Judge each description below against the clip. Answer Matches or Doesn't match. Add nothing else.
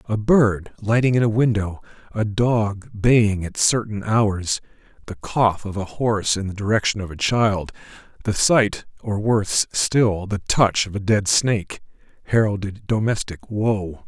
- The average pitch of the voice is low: Matches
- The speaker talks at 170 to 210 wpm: Doesn't match